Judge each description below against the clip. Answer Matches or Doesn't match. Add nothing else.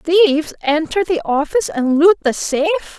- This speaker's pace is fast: Doesn't match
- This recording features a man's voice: Doesn't match